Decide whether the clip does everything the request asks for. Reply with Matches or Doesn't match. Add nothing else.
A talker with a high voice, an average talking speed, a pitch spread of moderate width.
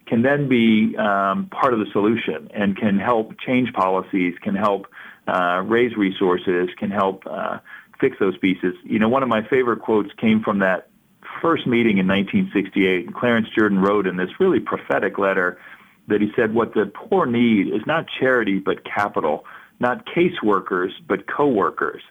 Doesn't match